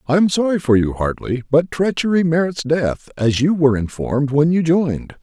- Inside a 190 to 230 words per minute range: Yes, average, 195 wpm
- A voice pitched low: No, medium, 150 Hz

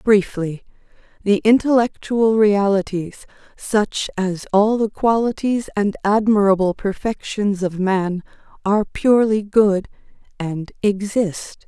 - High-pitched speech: Yes, high, 205 Hz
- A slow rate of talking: Yes, slow, 100 wpm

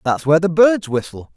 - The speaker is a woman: No, male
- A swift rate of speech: No, average, 175 wpm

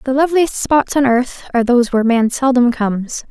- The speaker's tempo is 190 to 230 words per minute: Yes, average, 200 wpm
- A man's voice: No, female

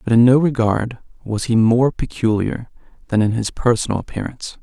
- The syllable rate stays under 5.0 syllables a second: No, 5.4 syllables/s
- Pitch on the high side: No, low, 115 Hz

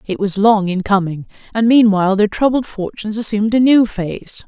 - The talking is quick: No, average, 190 wpm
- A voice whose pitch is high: Yes, high, 210 Hz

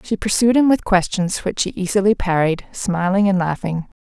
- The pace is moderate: Yes, average, 180 wpm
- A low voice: No, high, 195 Hz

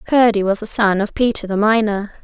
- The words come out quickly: Yes, fast, 215 wpm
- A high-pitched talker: Yes, high, 210 Hz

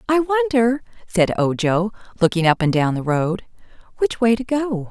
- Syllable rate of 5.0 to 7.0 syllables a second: No, 4.6 syllables/s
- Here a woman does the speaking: Yes, female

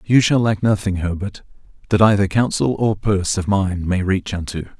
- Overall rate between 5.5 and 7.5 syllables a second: No, 5.1 syllables/s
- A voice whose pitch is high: No, low, 100 Hz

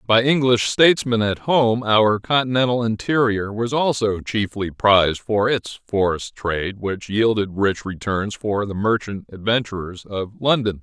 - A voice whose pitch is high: No, low, 110 Hz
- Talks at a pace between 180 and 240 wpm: No, average, 145 wpm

